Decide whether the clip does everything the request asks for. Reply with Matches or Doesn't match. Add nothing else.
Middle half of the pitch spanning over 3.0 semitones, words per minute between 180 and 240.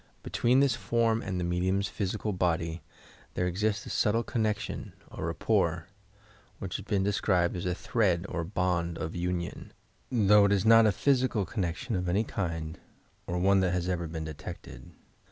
Doesn't match